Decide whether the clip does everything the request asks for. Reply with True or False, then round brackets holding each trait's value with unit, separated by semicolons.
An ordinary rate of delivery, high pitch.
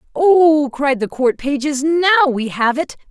True (175 wpm; 290 Hz)